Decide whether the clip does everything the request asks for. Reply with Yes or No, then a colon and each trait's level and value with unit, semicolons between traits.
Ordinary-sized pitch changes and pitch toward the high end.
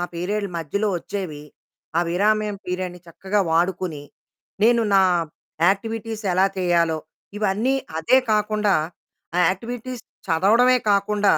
Yes: average, 3.2 semitones; high, 200 Hz